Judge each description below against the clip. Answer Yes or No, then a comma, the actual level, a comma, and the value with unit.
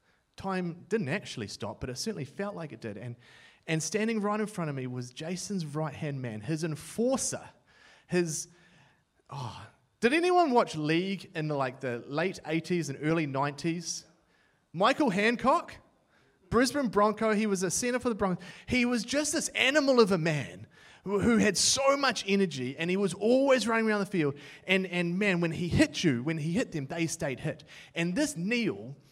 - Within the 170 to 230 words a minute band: Yes, average, 185 wpm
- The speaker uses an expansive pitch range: Yes, wide, 5.9 semitones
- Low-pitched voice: No, medium, 175 Hz